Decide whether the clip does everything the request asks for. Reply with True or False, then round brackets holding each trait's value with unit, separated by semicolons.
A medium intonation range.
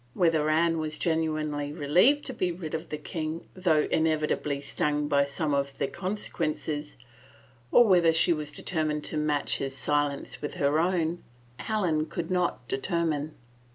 False (2.3 semitones)